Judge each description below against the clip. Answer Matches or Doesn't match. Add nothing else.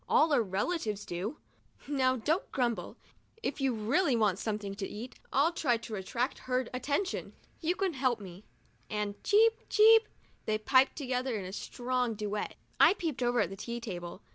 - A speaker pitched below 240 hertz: Doesn't match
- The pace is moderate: Matches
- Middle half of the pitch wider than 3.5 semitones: Matches